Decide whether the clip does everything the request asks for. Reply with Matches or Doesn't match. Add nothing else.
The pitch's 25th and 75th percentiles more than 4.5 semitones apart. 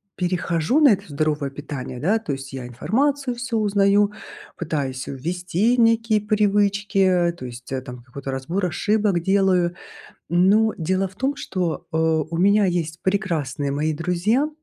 Matches